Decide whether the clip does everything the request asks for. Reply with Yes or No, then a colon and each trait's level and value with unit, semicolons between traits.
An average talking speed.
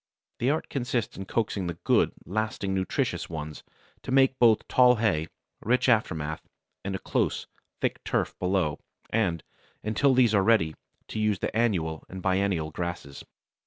Yes: average, 155 wpm